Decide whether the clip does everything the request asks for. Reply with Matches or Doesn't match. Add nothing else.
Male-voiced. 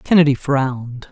Doesn't match